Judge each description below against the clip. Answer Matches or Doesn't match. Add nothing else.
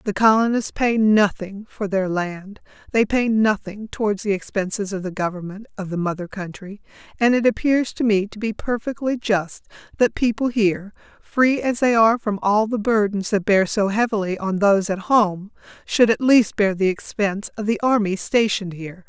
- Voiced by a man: Doesn't match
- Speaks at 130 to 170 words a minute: Doesn't match